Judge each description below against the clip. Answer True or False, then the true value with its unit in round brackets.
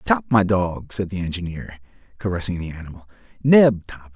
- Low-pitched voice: True (90 Hz)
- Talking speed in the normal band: True (160 wpm)